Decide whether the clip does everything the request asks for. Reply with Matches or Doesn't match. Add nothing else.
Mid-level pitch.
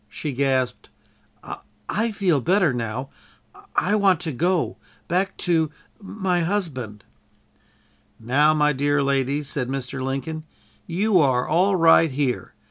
Matches